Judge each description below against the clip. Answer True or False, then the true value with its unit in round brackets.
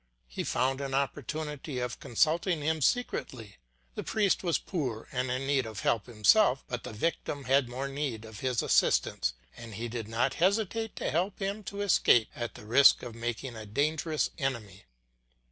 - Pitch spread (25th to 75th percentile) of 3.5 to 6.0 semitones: True (5.2 semitones)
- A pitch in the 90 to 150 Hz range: True (135 Hz)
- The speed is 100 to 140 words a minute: False (175 wpm)